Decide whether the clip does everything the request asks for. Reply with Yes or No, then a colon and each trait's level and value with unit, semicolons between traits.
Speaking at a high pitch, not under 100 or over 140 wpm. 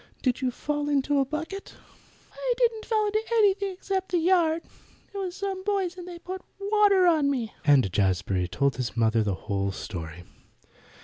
No: very high, 330 Hz; average, 175 wpm